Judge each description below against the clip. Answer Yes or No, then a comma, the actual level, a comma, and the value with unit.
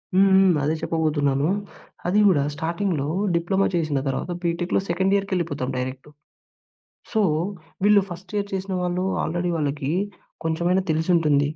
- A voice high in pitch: No, medium, 170 Hz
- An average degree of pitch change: Yes, average, 4.1 semitones